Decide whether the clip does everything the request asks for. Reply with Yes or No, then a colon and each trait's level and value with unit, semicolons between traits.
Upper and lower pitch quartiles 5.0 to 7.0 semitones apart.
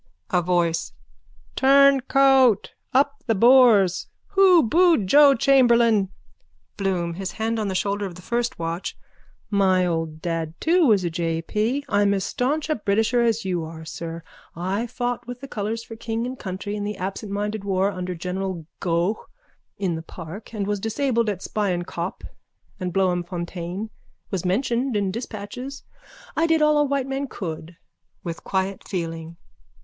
Yes: wide, 5.4 semitones